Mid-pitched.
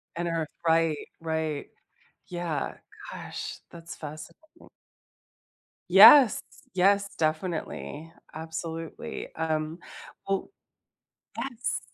Yes: medium, 165 Hz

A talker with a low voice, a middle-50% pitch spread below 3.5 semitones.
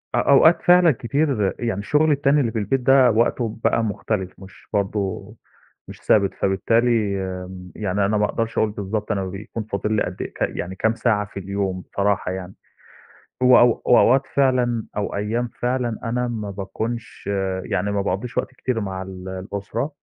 No: low, 105 Hz; average, 3.8 semitones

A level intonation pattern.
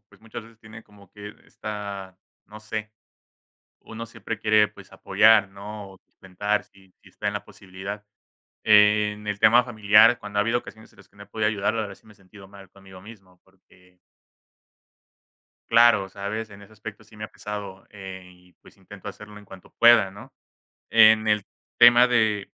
Yes: narrow, 1.9 semitones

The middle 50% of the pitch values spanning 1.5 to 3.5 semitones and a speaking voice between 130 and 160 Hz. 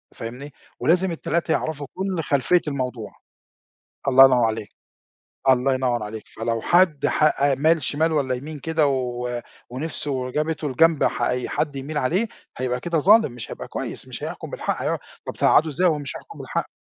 No: average, 4.1 semitones; medium, 140 Hz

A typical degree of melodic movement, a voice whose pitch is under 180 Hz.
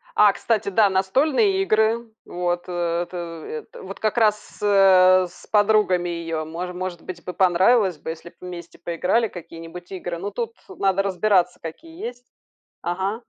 No: average, 3.4 semitones; medium, 185 Hz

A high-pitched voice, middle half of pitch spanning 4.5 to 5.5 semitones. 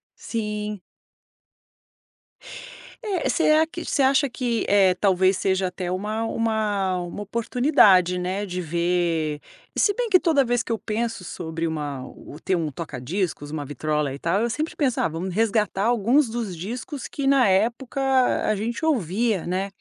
Yes: high, 205 Hz; average, 5.2 semitones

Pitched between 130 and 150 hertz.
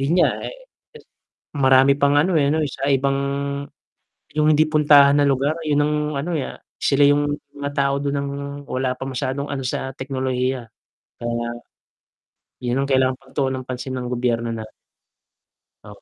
Yes: low, 135 Hz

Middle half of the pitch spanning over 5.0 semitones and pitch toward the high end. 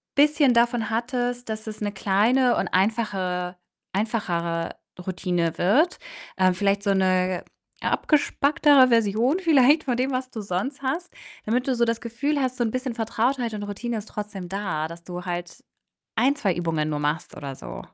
Yes: wide, 5.4 semitones; high, 220 Hz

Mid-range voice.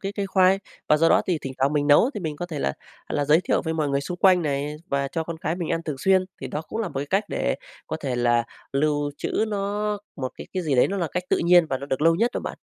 Yes: medium, 160 Hz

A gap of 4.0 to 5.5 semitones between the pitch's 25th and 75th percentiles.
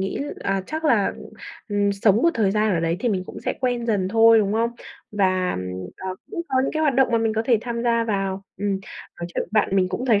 No: average, 3.3 semitones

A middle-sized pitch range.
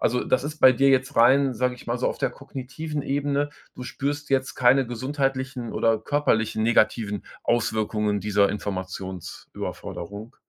Yes: average, 3.9 semitones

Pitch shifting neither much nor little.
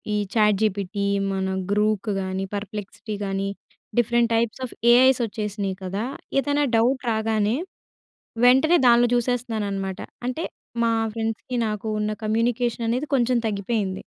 Yes: average, 3.0 semitones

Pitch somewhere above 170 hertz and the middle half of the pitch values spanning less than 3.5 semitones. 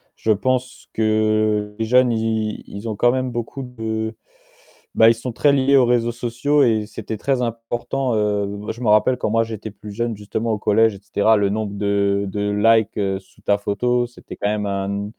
No: low, 110 Hz; narrow, 2.6 semitones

